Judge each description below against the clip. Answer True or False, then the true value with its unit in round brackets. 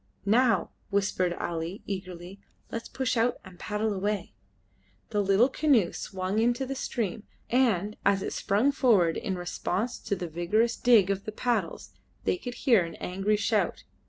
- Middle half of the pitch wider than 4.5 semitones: False (4.1 semitones)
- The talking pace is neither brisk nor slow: True (160 wpm)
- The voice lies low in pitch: False (205 Hz)